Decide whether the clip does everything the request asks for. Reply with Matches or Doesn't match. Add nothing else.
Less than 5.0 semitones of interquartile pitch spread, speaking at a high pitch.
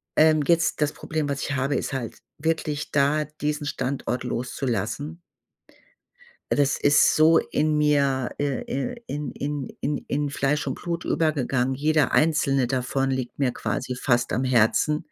Doesn't match